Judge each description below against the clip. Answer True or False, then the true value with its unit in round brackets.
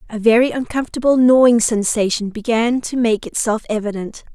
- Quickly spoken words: False (140 wpm)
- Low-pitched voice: False (230 Hz)